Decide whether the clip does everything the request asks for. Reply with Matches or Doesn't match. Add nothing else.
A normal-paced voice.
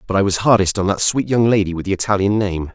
Doesn't match